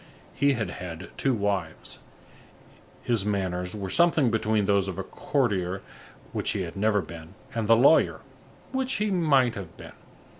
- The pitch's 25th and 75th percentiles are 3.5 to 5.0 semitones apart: No, wide, 5.5 semitones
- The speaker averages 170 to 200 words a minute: No, average, 155 wpm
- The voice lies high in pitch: No, low, 105 Hz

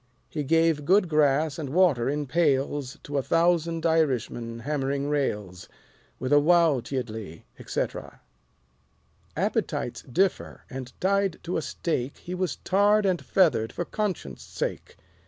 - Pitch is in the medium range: Yes, medium, 150 Hz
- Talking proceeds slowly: Yes, slow, 130 wpm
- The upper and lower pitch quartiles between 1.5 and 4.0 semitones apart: No, average, 4.7 semitones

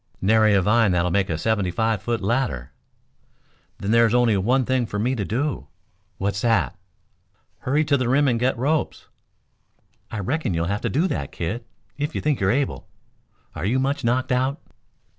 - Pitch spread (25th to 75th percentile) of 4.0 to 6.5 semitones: Yes, average, 4.7 semitones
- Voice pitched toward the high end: No, low, 115 Hz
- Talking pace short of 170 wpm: No, average, 185 wpm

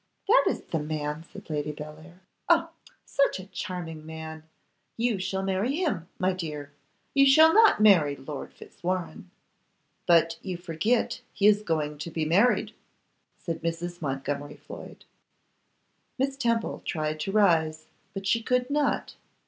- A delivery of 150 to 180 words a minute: No, average, 140 wpm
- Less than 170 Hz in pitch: No, medium, 175 Hz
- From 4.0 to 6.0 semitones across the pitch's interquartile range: Yes, average, 5.2 semitones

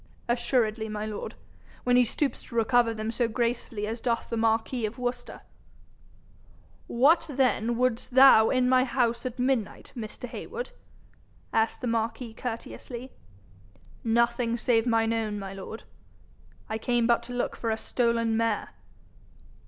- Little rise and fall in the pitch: Yes, narrow, 1.8 semitones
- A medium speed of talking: Yes, average, 145 wpm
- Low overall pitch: No, high, 235 Hz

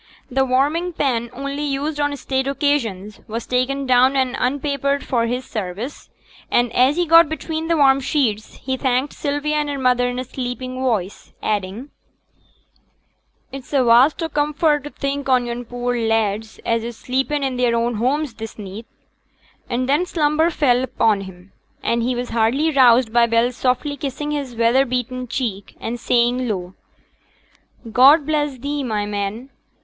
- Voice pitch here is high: Yes, very high, 255 Hz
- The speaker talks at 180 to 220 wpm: No, average, 165 wpm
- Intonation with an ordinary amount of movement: Yes, average, 3.4 semitones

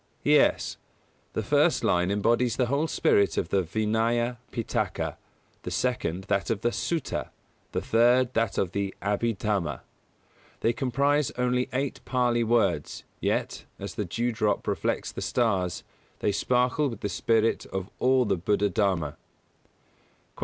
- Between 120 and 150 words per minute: Yes, average, 145 wpm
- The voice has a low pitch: Yes, low, 115 Hz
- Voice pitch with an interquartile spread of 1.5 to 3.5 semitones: No, average, 3.9 semitones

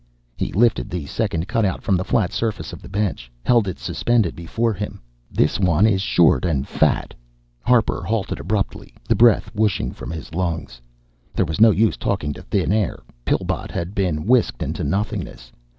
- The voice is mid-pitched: No, very low, 95 Hz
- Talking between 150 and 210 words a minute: Yes, average, 180 wpm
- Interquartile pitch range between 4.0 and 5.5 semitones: Yes, average, 4.9 semitones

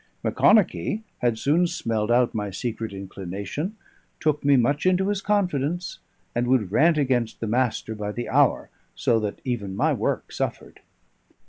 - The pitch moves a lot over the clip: Yes, wide, 6.5 semitones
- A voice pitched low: Yes, low, 125 Hz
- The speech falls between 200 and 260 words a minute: No, average, 150 wpm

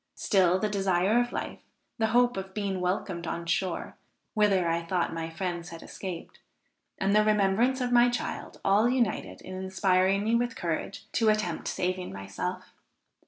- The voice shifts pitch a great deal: No, average, 3.3 semitones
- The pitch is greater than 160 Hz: Yes, high, 190 Hz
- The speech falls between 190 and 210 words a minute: No, average, 165 wpm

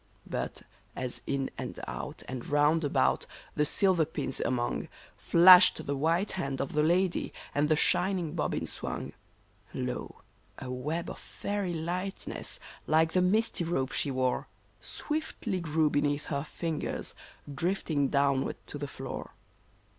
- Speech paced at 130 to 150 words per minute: Yes, average, 140 wpm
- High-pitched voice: No, medium, 155 Hz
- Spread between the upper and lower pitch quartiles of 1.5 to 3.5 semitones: No, average, 4.2 semitones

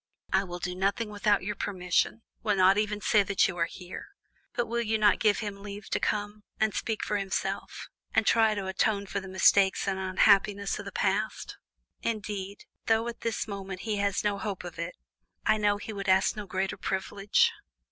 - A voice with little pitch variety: Yes, narrow, 1.8 semitones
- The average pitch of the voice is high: Yes, high, 200 Hz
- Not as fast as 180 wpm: No, average, 200 wpm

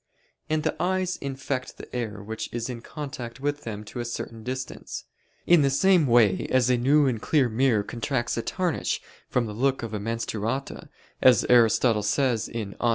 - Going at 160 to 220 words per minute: Yes, average, 185 wpm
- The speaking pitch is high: No, low, 125 Hz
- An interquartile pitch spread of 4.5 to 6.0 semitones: No, average, 3.3 semitones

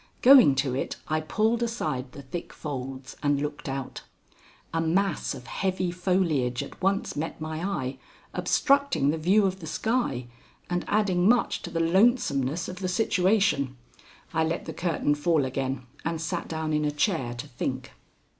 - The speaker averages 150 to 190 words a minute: Yes, average, 165 wpm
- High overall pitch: No, medium, 160 Hz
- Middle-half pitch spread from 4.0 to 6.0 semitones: Yes, wide, 5.5 semitones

